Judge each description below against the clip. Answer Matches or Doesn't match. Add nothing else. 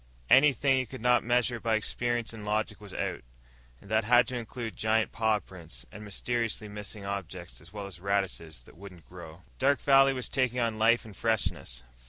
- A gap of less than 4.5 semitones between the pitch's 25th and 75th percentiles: Matches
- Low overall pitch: Matches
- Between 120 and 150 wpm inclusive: Doesn't match